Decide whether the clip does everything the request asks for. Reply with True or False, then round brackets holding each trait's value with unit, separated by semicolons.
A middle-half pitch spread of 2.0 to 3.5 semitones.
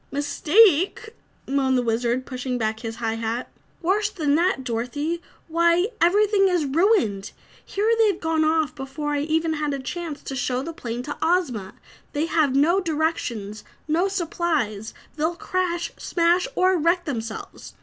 False (5.5 semitones)